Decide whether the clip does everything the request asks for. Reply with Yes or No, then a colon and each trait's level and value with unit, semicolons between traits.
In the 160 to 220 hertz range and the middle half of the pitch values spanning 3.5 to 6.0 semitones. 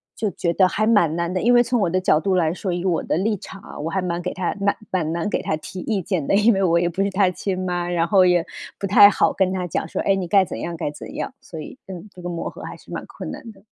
No: medium, 185 Hz; narrow, 2.5 semitones